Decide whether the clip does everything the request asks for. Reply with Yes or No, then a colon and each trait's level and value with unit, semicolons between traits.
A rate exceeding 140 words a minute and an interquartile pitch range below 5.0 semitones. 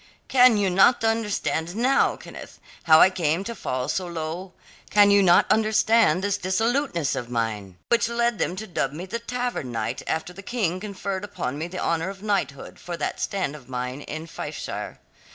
No: average, 185 wpm; wide, 5.5 semitones